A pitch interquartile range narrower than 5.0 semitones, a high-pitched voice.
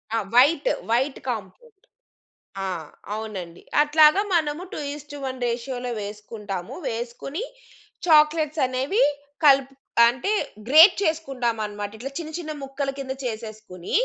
No: average, 5.3 semitones; very high, 265 Hz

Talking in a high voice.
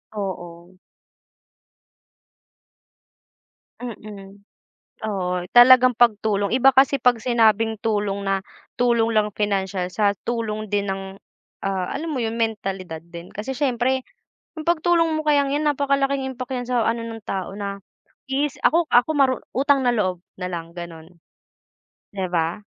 Yes: high, 220 Hz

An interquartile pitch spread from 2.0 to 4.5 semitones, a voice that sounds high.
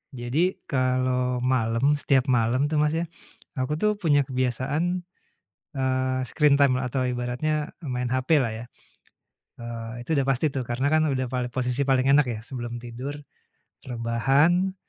No: average, 2.8 semitones; low, 130 Hz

